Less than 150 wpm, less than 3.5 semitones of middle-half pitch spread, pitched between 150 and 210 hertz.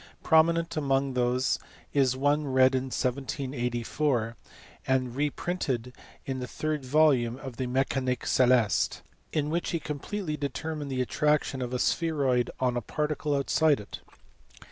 No: slow, 135 wpm; average, 3.0 semitones; low, 135 Hz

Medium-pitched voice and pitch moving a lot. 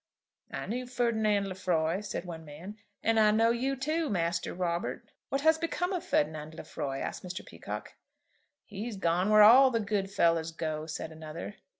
No: high, 195 Hz; wide, 5.8 semitones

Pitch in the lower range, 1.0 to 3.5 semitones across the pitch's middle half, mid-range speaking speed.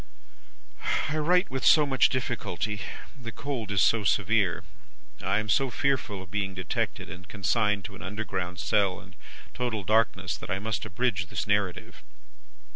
No: low, 105 Hz; average, 3.9 semitones; average, 155 wpm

